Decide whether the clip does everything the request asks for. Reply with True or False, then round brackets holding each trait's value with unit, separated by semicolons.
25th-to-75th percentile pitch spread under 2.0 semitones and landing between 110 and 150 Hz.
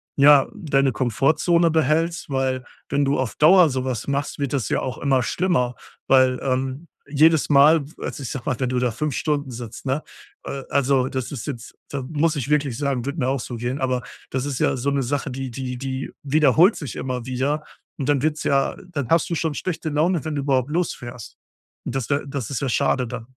False (2.6 semitones; 140 Hz)